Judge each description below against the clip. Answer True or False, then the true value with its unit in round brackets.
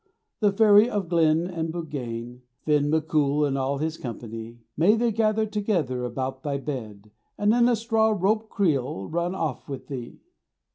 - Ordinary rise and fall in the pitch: False (7.6 semitones)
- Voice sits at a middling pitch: True (160 Hz)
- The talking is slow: False (175 wpm)